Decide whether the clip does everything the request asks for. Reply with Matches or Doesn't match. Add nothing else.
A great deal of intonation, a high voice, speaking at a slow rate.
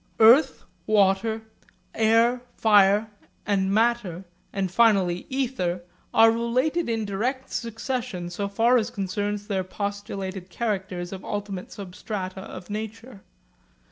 Doesn't match